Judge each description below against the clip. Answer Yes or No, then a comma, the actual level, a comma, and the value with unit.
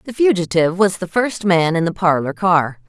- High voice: No, medium, 180 Hz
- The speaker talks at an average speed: No, fast, 210 wpm